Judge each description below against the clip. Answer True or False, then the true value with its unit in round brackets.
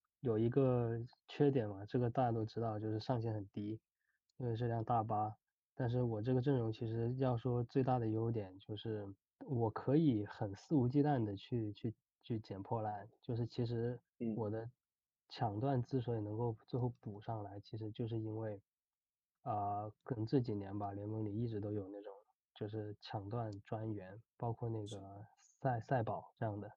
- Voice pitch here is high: False (115 Hz)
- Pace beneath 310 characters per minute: True (260 characters per minute)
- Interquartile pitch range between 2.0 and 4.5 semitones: True (2.5 semitones)